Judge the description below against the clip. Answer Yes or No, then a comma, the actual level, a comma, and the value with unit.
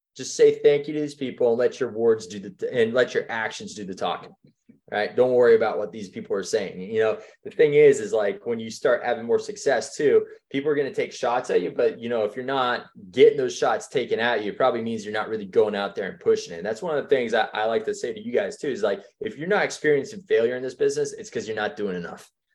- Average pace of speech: No, fast, 285 wpm